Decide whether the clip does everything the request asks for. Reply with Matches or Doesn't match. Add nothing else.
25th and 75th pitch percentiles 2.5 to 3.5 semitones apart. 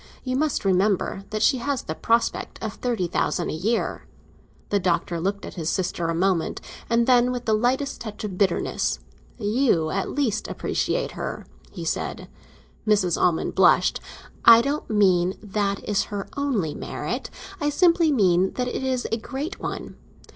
Doesn't match